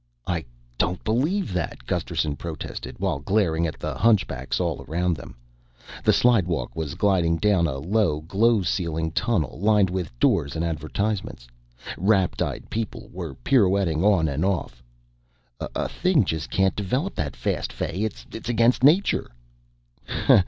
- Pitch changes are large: No, average, 4.9 semitones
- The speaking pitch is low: Yes, very low, 90 Hz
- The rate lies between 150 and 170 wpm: No, average, 140 wpm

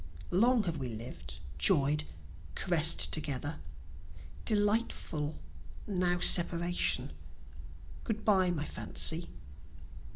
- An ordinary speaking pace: No, slow, 85 wpm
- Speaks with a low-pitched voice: No, medium, 175 Hz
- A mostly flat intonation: No, average, 4.7 semitones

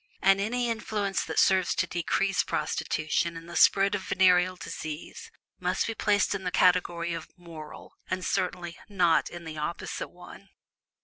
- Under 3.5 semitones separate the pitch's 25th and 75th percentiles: Yes, narrow, 2.4 semitones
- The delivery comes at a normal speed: Yes, average, 160 wpm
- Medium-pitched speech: Yes, medium, 180 Hz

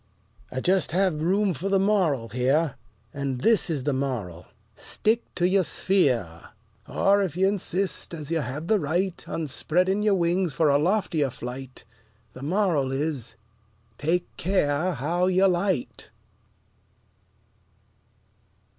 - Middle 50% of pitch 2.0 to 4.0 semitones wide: No, wide, 5.5 semitones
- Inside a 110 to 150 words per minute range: Yes, slow, 135 wpm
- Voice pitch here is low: No, medium, 165 Hz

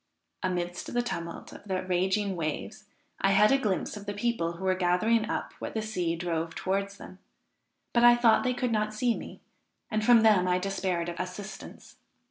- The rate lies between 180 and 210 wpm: Yes, average, 190 wpm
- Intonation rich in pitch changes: No, average, 3.4 semitones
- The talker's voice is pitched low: No, high, 195 Hz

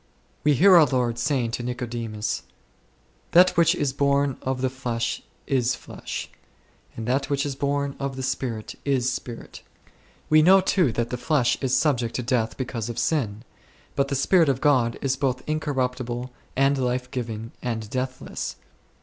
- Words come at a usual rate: Yes, average, 165 wpm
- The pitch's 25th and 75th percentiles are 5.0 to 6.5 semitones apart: No, average, 2.8 semitones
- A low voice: Yes, low, 130 Hz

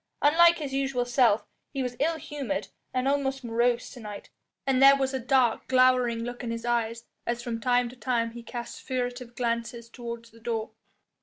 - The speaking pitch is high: Yes, high, 245 Hz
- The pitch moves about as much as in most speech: No, narrow, 2.2 semitones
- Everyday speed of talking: Yes, average, 185 wpm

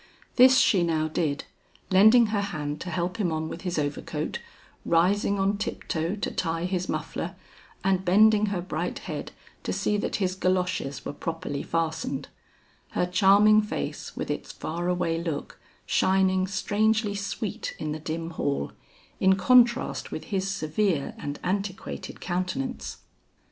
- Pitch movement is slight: No, average, 3.7 semitones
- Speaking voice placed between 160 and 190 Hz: Yes, medium, 185 Hz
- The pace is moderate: Yes, average, 150 wpm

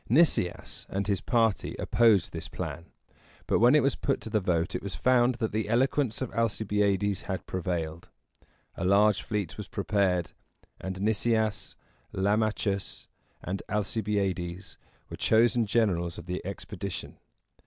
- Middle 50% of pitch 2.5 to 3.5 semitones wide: Yes, average, 3.0 semitones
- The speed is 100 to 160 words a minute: Yes, average, 145 wpm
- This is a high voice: No, low, 100 Hz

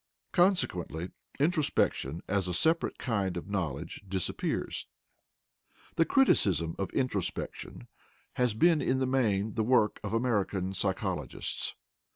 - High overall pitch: No, low, 100 Hz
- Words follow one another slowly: Yes, slow, 115 wpm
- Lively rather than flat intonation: Yes, wide, 6.0 semitones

